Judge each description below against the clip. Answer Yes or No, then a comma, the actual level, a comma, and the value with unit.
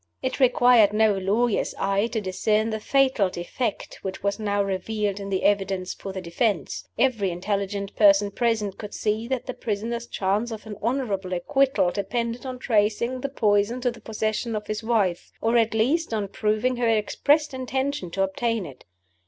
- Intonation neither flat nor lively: Yes, average, 3.2 semitones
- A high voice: Yes, high, 215 Hz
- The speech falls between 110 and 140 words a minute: No, average, 175 wpm